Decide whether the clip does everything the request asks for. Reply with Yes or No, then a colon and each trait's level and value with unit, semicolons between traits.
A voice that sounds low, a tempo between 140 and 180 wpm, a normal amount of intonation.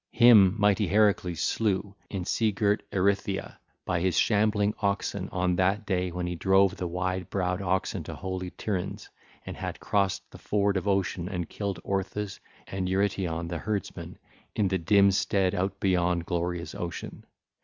No: very low, 95 Hz; average, 160 wpm; narrow, 2.0 semitones